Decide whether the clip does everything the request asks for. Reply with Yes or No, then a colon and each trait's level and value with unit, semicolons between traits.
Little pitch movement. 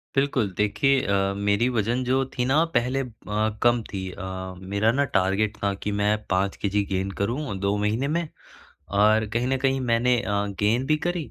No: average, 4.3 semitones